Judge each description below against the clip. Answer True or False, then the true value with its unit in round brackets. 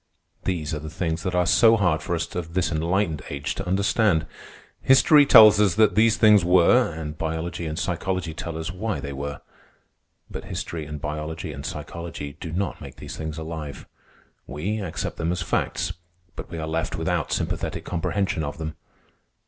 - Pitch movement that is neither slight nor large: True (3.2 semitones)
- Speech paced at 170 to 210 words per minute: True (180 wpm)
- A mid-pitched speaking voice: False (85 Hz)